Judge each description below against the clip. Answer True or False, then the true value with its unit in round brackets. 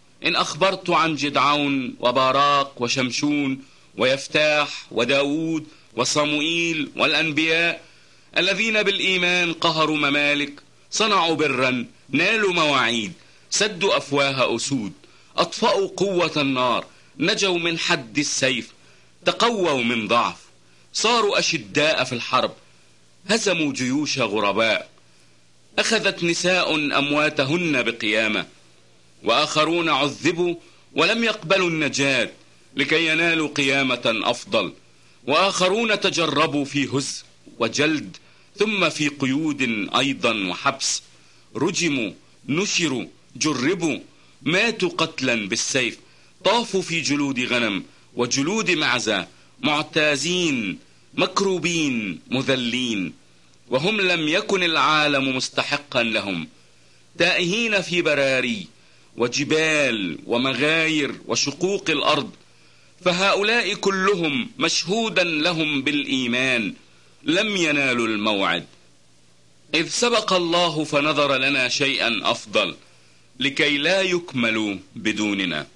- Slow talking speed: True (85 wpm)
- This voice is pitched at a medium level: True (145 Hz)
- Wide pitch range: True (5.8 semitones)